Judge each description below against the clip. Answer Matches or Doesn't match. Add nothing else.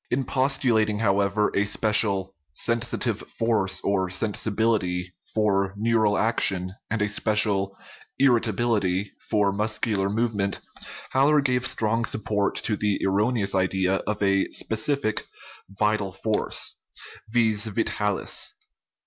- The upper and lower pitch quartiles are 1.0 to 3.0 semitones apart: Matches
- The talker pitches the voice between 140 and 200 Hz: Doesn't match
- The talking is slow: Matches